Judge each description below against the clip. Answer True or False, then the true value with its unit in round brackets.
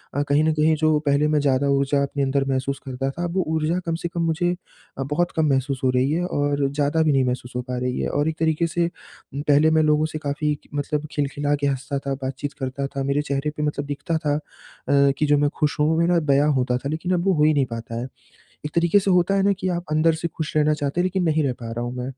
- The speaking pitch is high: False (145 Hz)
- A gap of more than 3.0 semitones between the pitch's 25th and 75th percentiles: False (2.5 semitones)